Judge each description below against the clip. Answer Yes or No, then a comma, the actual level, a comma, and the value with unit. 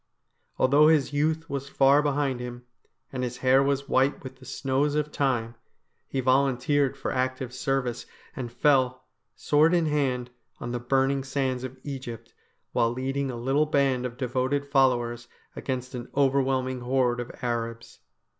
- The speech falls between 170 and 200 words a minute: No, average, 155 wpm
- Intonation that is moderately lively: No, narrow, 1.9 semitones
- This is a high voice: No, low, 130 Hz